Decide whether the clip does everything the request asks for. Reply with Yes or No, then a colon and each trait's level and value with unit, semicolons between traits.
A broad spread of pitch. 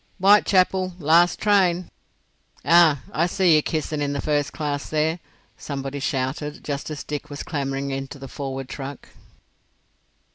No: average, 3.7 semitones